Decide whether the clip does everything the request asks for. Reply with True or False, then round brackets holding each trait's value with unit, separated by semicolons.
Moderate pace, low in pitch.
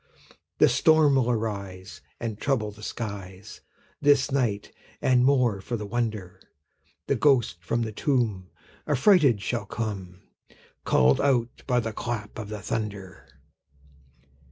False (130 wpm; 115 Hz)